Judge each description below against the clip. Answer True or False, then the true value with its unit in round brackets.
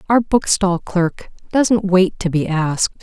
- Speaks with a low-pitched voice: False (190 Hz)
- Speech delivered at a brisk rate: False (160 wpm)